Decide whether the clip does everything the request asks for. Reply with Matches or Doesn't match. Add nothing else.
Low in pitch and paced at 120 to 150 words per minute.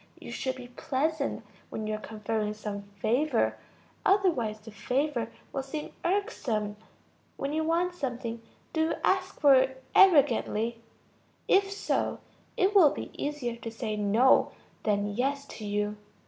Doesn't match